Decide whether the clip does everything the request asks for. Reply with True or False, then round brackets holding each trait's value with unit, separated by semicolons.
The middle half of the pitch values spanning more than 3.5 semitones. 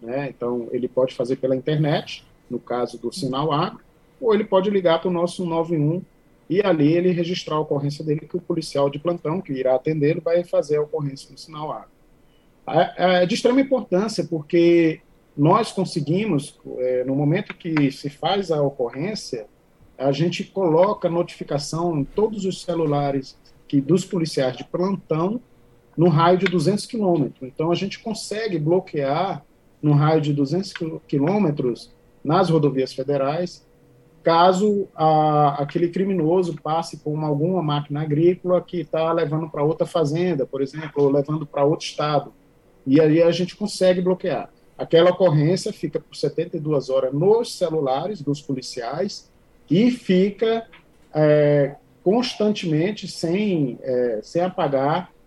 True (4.0 semitones)